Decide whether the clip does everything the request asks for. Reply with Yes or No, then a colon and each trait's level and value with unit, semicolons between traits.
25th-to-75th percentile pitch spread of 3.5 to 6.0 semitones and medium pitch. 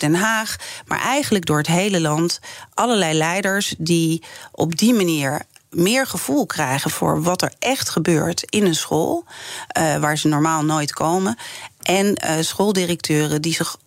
Yes: average, 4.2 semitones; medium, 170 Hz